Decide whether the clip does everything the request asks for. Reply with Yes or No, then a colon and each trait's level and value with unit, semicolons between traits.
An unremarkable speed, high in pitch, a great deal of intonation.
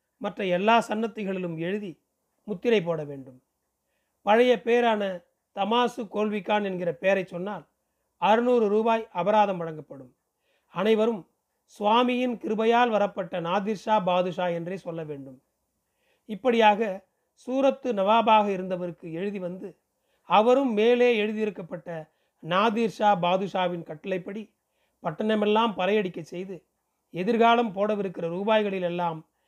No: average, 90 wpm; high, 205 Hz; average, 3.9 semitones